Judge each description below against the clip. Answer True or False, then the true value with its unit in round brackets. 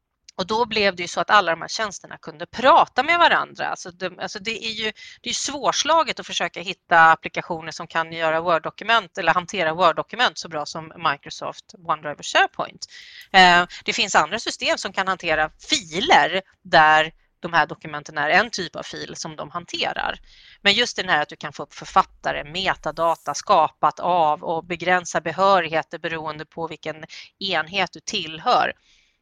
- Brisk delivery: False (175 wpm)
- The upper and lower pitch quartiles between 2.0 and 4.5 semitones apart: True (3.9 semitones)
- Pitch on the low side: False (175 Hz)